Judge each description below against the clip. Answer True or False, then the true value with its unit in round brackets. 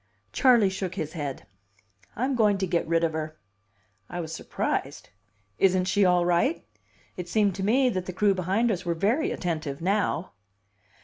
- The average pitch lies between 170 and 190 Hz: True (185 Hz)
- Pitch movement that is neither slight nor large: True (3.5 semitones)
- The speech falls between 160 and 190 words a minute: True (170 wpm)